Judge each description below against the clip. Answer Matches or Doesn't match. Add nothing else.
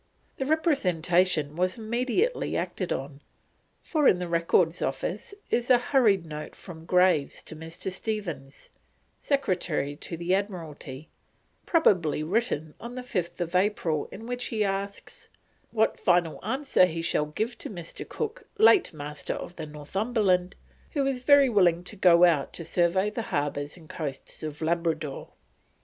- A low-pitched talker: Doesn't match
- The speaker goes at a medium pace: Matches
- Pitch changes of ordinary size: Doesn't match